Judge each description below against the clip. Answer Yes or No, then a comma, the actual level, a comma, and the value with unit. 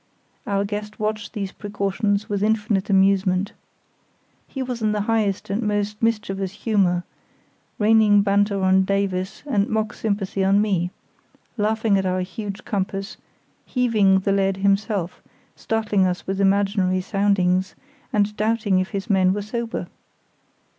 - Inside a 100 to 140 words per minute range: Yes, slow, 135 wpm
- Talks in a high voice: Yes, high, 200 Hz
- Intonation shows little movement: Yes, narrow, 1.7 semitones